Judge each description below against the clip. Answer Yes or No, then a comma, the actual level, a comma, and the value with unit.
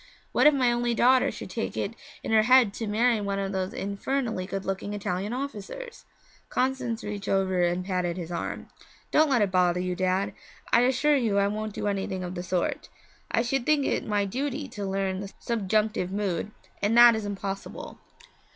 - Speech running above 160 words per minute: Yes, average, 190 wpm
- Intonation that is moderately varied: Yes, average, 4.0 semitones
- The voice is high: Yes, high, 205 Hz